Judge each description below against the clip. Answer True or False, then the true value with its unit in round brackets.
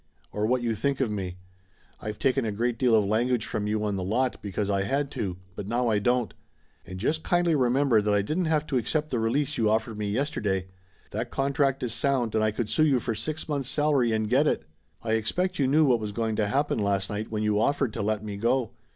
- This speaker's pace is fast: True (240 wpm)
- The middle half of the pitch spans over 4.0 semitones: True (4.5 semitones)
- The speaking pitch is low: True (115 Hz)